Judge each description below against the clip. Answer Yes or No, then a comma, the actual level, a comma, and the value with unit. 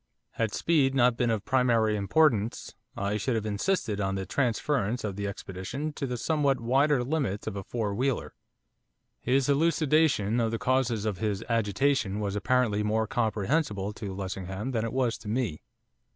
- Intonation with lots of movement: No, average, 4.5 semitones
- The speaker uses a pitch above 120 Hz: No, low, 115 Hz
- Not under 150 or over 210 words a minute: Yes, average, 165 wpm